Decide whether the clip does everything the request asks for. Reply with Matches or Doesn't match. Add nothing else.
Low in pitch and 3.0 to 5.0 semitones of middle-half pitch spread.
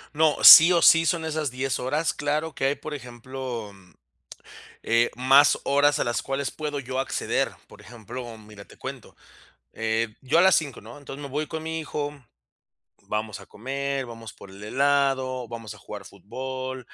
Matches